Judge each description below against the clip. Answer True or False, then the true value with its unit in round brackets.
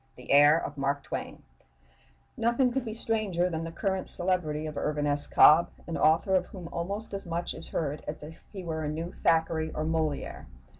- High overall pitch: False (165 Hz)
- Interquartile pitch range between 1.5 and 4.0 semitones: True (3.6 semitones)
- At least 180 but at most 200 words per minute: True (195 wpm)